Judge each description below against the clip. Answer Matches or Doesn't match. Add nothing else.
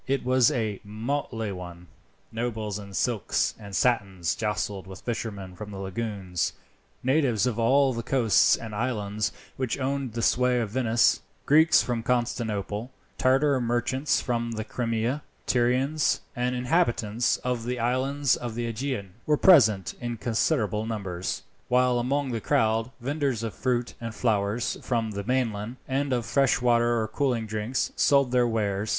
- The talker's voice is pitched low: Matches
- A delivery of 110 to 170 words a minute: Matches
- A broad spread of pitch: Doesn't match